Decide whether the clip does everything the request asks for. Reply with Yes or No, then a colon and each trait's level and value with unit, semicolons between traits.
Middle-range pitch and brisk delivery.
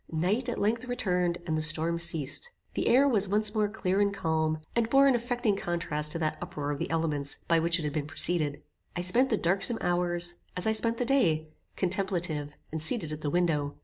Yes: medium, 175 Hz; fast, 215 wpm